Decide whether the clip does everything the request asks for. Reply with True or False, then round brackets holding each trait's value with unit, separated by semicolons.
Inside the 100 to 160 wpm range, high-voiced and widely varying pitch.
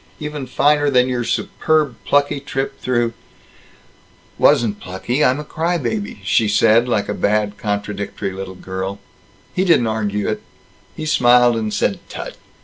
False (150 wpm; 120 Hz; 5.7 semitones)